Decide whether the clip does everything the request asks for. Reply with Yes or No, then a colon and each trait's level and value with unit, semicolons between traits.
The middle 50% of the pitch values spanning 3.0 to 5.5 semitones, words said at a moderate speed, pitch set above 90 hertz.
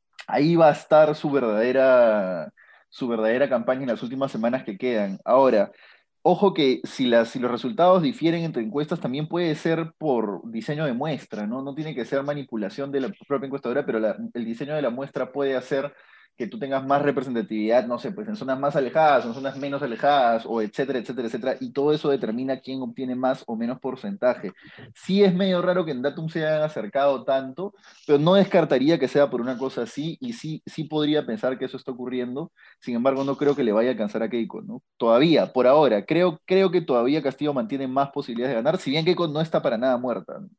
No: average, 3.7 semitones; fast, 215 wpm; medium, 140 Hz